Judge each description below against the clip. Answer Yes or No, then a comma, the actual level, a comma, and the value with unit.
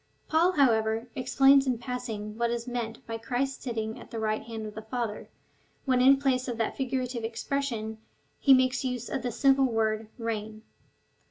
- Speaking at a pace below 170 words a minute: No, average, 175 wpm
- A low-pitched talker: No, high, 240 Hz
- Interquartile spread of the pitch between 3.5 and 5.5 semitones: No, average, 2.8 semitones